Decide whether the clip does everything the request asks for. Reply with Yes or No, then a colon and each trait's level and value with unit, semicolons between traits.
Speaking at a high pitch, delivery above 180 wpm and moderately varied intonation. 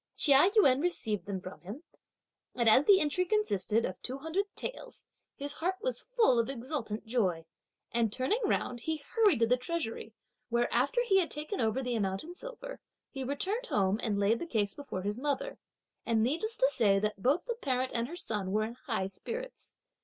No: very high, 255 Hz; average, 195 wpm; wide, 8.1 semitones